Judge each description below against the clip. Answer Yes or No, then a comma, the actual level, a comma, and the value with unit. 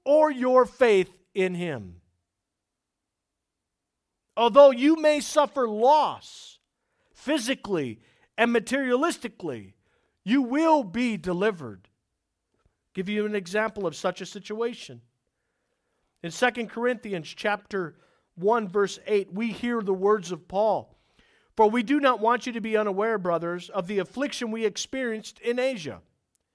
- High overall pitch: Yes, high, 215 Hz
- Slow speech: Yes, slow, 125 wpm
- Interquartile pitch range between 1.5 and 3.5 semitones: No, average, 5.3 semitones